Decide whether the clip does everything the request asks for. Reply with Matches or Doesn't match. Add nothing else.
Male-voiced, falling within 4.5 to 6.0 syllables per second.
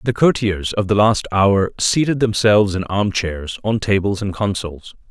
Matches